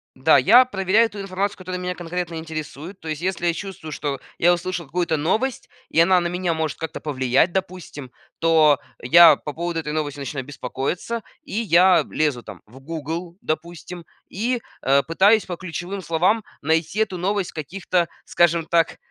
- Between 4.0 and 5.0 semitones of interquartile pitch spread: No, average, 3.0 semitones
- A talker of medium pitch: Yes, medium, 170 Hz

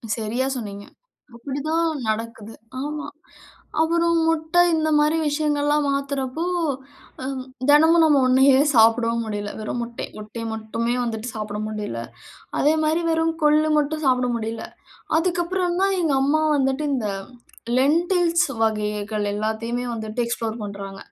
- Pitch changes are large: Yes, wide, 5.9 semitones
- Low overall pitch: No, very high, 265 Hz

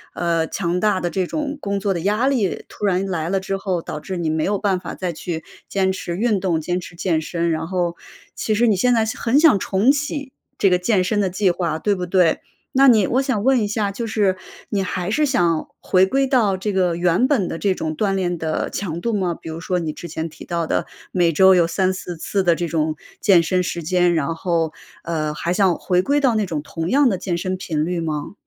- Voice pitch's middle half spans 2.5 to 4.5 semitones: Yes, average, 3.4 semitones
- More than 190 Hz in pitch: No, medium, 185 Hz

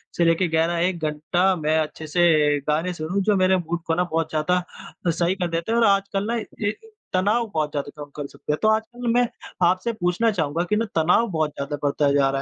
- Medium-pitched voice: Yes, medium, 170 Hz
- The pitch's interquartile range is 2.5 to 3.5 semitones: No, average, 4.1 semitones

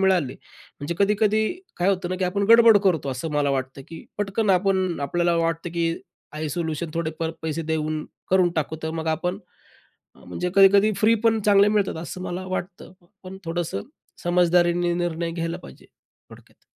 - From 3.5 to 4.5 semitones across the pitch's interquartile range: No, average, 3.0 semitones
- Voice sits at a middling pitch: Yes, medium, 175 Hz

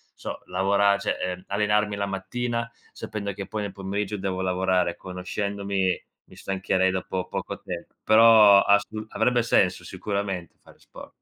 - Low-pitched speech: Yes, low, 100 Hz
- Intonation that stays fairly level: Yes, narrow, 1.9 semitones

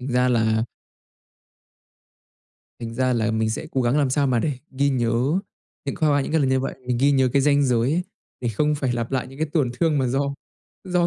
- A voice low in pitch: Yes, low, 130 Hz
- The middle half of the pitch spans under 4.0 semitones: Yes, average, 3.1 semitones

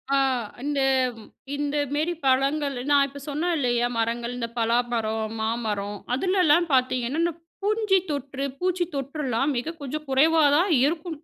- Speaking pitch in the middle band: No, very high, 280 Hz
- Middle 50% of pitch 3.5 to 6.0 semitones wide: Yes, average, 4.9 semitones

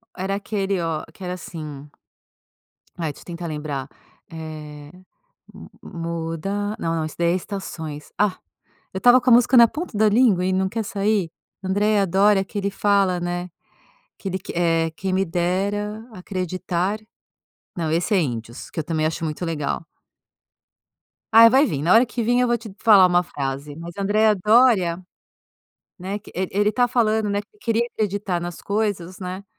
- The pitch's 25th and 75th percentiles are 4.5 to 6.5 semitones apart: No, average, 3.9 semitones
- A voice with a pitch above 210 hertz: No, high, 190 Hz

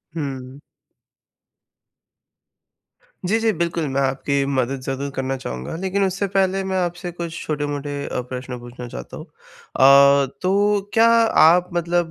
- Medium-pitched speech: Yes, medium, 160 Hz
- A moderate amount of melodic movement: No, wide, 5.9 semitones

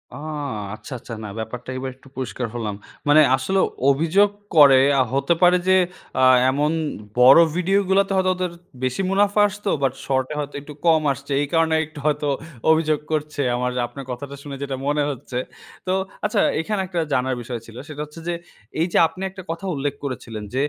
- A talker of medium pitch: Yes, medium, 145 Hz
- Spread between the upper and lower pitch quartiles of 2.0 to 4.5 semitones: No, average, 4.9 semitones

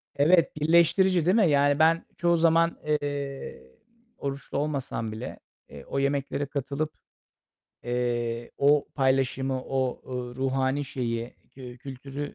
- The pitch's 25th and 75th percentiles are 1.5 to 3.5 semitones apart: Yes, average, 2.9 semitones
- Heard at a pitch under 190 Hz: Yes, medium, 140 Hz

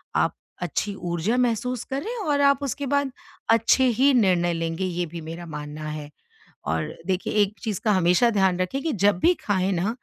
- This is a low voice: No, high, 190 Hz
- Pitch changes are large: Yes, wide, 6.4 semitones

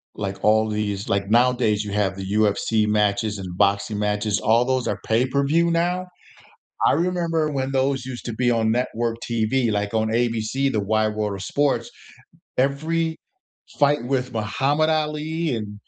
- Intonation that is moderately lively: Yes, average, 4.6 semitones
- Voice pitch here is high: No, low, 115 Hz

